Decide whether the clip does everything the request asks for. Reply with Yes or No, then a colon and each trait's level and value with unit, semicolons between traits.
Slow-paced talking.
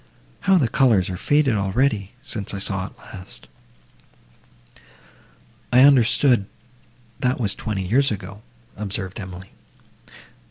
Yes: slow, 110 wpm